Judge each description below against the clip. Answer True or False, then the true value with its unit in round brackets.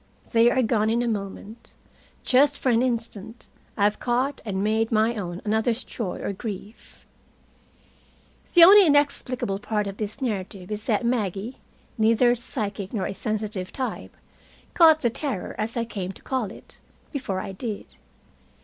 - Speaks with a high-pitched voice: True (225 Hz)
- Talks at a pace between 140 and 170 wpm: True (160 wpm)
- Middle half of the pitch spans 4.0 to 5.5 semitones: False (3.5 semitones)